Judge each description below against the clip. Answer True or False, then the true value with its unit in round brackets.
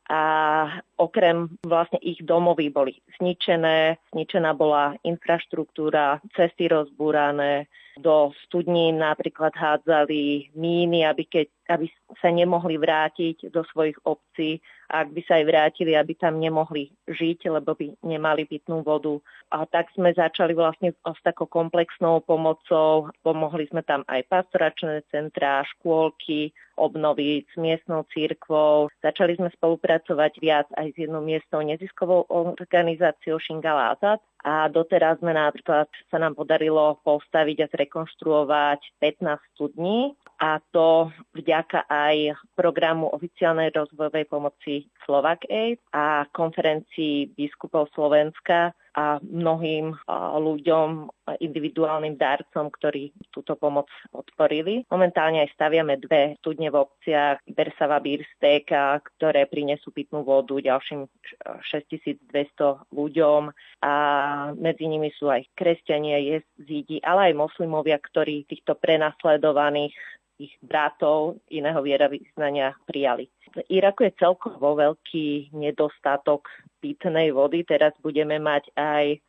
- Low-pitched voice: False (155 Hz)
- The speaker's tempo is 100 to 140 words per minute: True (115 wpm)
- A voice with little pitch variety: True (1.9 semitones)